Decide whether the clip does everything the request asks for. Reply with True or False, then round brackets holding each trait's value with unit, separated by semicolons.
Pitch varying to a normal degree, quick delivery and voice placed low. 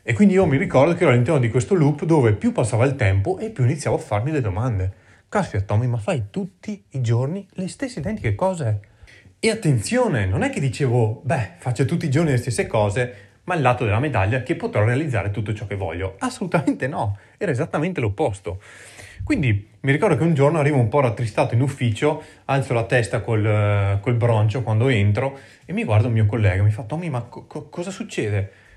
False (6.2 semitones; 210 wpm; 125 Hz)